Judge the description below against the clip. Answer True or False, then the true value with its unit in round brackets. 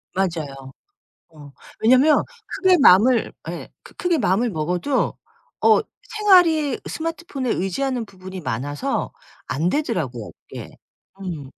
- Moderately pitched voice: False (195 Hz)